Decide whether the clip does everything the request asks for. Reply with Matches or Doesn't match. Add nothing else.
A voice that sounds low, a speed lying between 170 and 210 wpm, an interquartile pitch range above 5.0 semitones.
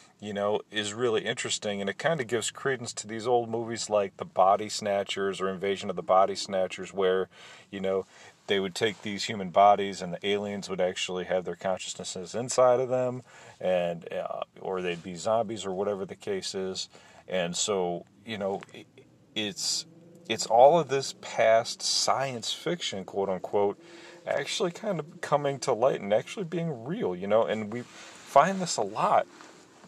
Matches